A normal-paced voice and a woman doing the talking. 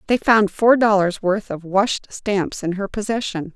Yes: average, 185 wpm; female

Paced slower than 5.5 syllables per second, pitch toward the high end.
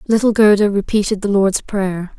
Yes: 4.9 syllables/s; high, 200 Hz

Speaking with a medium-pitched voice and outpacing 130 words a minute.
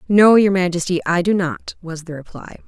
Yes: medium, 180 Hz; average, 200 wpm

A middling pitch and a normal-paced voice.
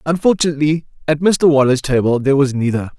Yes: medium, 145 Hz; average, 160 wpm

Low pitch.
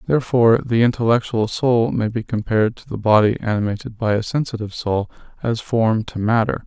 Yes: low, 110 Hz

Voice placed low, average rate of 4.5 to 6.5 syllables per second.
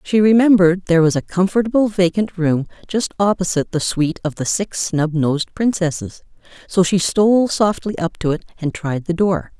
No: medium, 180 Hz; 5.4 syllables/s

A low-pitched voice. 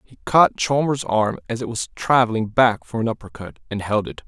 Yes: low, 120 Hz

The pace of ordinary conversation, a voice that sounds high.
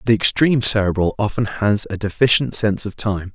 No: average, 180 wpm; low, 105 Hz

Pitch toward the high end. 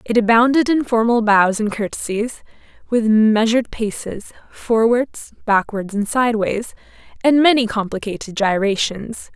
Yes: high, 225 Hz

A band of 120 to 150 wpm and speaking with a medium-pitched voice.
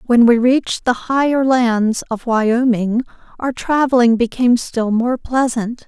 No: average, 145 wpm; high, 240 Hz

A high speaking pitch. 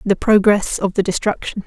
Yes: high, 200 Hz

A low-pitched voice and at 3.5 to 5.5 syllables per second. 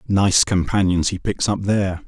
Yes: very low, 95 Hz; 4.7 syllables/s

